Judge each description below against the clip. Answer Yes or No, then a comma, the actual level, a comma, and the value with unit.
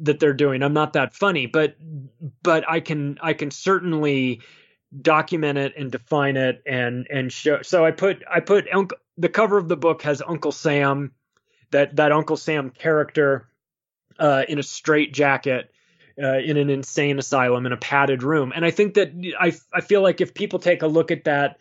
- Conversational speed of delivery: Yes, average, 195 wpm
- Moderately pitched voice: Yes, medium, 150 Hz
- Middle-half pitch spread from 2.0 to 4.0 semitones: Yes, average, 3.1 semitones